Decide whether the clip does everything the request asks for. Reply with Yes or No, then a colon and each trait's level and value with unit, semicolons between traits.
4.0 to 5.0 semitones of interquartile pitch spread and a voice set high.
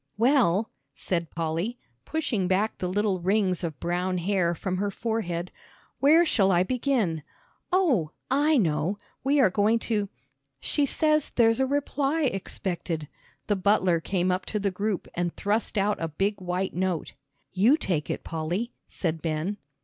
Yes: average, 4.7 semitones; high, 195 Hz